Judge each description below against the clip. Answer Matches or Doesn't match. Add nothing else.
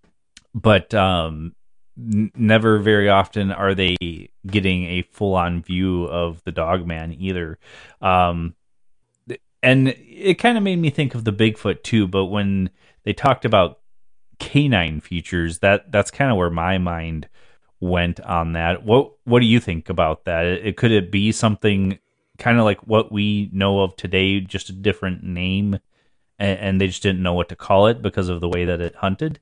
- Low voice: Matches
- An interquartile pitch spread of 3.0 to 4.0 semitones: Matches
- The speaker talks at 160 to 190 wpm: Matches